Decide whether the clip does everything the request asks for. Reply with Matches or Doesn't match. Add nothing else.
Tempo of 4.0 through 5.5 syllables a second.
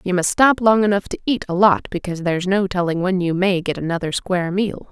Doesn't match